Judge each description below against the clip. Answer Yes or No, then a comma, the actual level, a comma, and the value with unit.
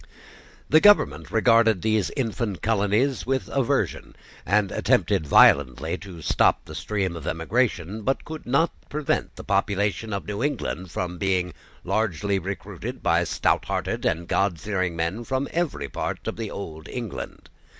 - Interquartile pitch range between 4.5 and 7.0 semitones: Yes, average, 4.8 semitones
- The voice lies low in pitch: Yes, low, 100 Hz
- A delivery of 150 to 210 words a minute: No, average, 140 wpm